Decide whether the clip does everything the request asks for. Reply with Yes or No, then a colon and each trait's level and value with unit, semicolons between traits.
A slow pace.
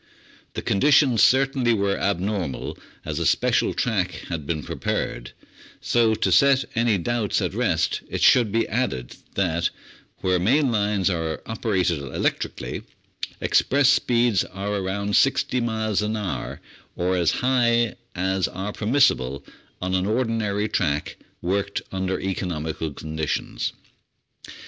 Yes: slow, 125 wpm